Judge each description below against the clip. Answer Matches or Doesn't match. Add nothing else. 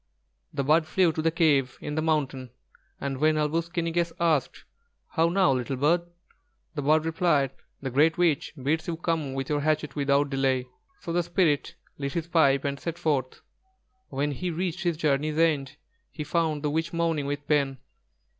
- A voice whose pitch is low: Doesn't match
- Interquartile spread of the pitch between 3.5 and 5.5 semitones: Doesn't match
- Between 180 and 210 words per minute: Matches